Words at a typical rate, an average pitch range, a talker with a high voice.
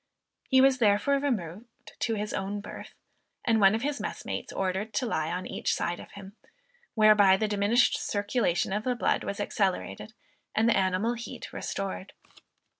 Yes: average, 165 wpm; average, 3.5 semitones; high, 210 Hz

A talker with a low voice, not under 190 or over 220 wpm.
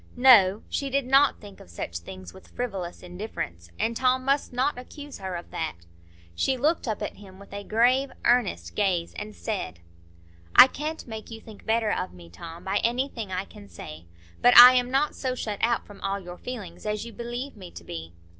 No: high, 215 Hz; average, 200 wpm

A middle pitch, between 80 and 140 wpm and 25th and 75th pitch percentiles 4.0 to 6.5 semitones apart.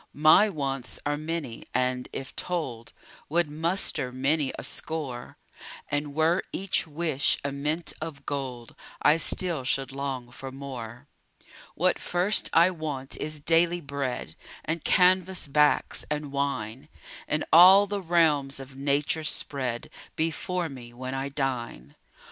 No: medium, 145 Hz; slow, 135 wpm; average, 3.5 semitones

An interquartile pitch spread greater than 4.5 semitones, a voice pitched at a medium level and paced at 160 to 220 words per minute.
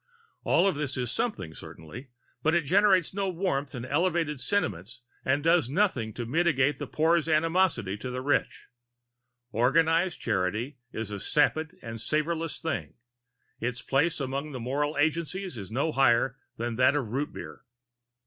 No: average, 5.1 semitones; medium, 145 Hz; average, 150 wpm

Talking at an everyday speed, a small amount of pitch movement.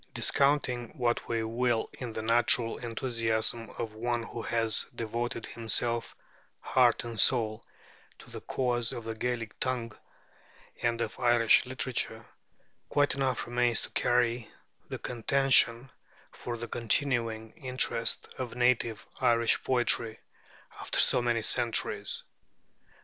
No: slow, 120 wpm; narrow, 1.3 semitones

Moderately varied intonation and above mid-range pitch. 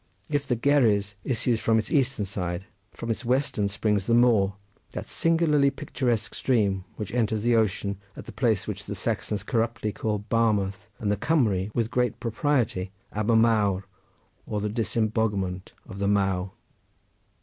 No: average, 3.0 semitones; low, 110 Hz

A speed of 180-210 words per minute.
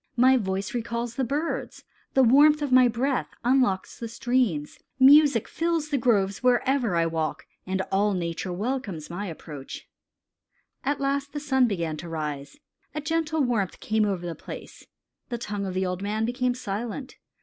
No: average, 165 wpm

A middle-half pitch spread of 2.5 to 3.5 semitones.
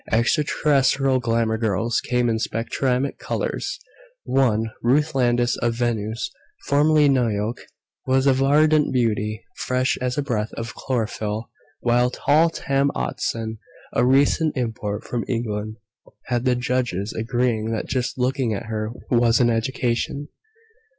Yes: average, 2.9 semitones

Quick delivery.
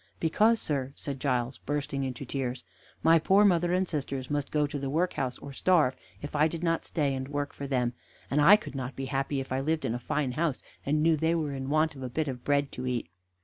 Yes: fast, 240 wpm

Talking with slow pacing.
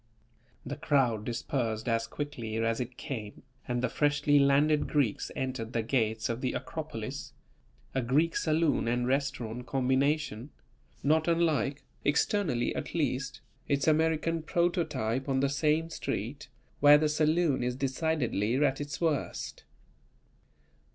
Yes: slow, 130 wpm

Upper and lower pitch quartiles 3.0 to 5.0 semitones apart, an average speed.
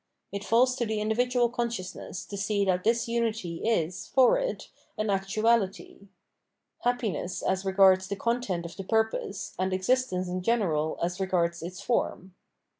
Yes: average, 4.0 semitones; average, 160 wpm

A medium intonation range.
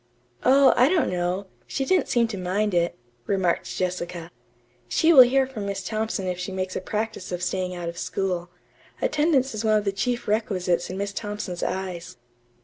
Yes: average, 4.0 semitones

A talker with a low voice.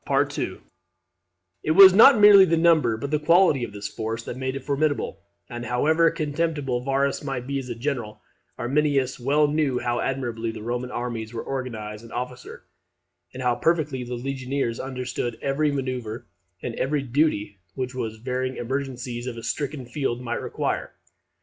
Yes: low, 130 Hz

